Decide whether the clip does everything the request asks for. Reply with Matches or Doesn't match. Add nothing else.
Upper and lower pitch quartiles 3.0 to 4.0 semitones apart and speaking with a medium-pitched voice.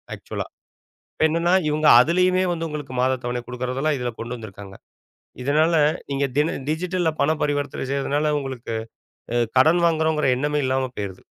Matches